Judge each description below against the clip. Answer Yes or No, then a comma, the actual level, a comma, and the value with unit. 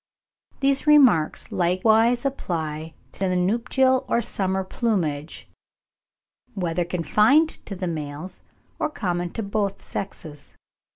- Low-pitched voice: No, high, 190 Hz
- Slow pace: Yes, slow, 110 wpm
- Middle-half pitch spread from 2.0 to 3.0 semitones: No, wide, 5.5 semitones